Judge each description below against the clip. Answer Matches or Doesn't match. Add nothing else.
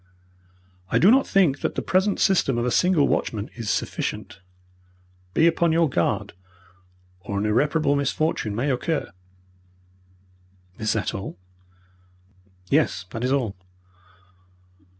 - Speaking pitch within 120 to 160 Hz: Matches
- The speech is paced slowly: Matches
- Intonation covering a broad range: Matches